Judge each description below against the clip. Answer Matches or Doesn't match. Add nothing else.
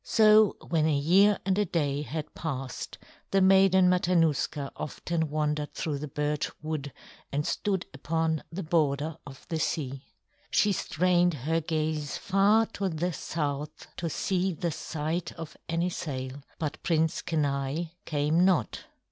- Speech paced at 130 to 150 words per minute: Matches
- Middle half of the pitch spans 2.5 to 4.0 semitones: Matches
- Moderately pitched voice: Matches